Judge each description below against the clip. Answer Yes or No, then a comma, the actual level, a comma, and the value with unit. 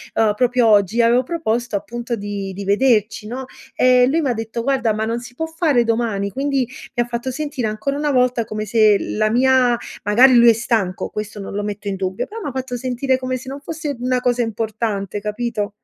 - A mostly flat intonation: No, average, 3.3 semitones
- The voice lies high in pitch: Yes, high, 235 Hz